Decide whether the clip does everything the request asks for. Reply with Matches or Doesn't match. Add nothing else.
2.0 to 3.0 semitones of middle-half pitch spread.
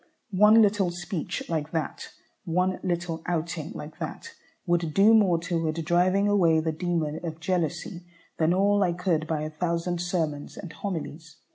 Matches